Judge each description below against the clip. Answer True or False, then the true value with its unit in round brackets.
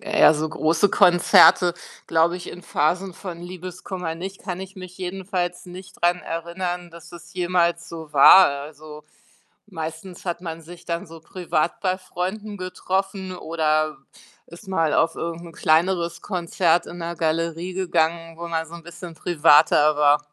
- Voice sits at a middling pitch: True (170 Hz)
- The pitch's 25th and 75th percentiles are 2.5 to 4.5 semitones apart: False (2.1 semitones)